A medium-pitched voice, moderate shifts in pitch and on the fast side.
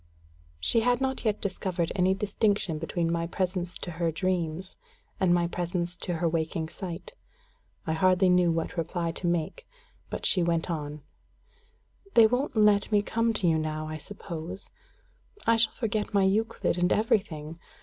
No: medium, 180 Hz; average, 3.5 semitones; average, 160 wpm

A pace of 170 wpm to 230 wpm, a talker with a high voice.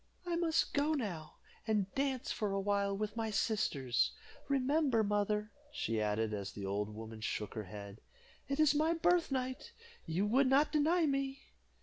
No: average, 160 wpm; high, 215 Hz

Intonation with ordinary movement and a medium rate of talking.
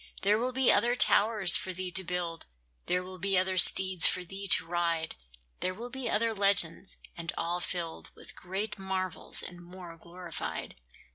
No: narrow, 2.3 semitones; average, 170 wpm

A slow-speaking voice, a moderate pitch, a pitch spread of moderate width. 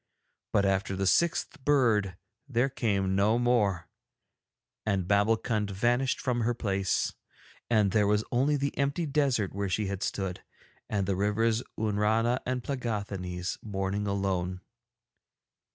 No: slow, 130 wpm; low, 105 Hz; average, 3.8 semitones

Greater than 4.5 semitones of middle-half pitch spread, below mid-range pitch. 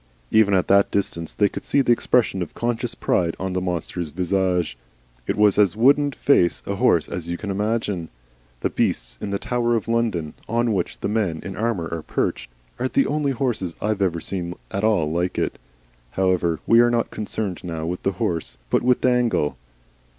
Yes: average, 5.0 semitones; low, 100 Hz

